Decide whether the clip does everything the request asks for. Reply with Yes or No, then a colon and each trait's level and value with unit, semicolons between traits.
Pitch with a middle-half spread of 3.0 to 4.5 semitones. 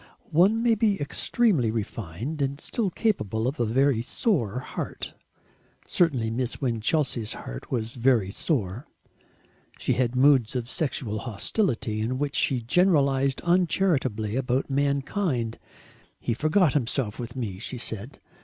No: average, 5.1 semitones